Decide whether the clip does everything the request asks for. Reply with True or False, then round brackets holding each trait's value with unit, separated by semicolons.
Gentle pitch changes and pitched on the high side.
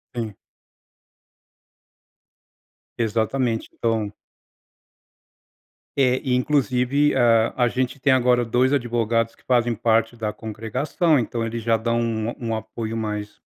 False (2.0 semitones; 115 Hz)